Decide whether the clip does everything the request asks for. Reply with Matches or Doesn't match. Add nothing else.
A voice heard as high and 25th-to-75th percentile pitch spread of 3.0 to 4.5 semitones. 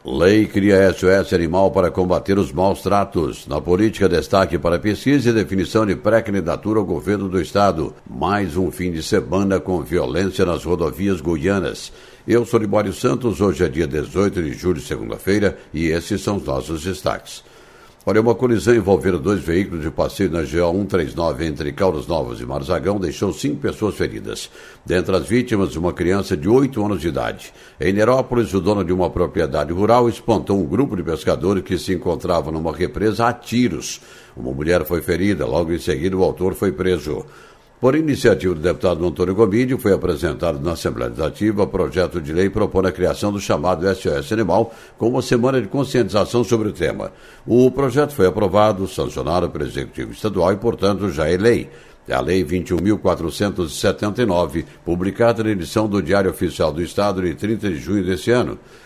Doesn't match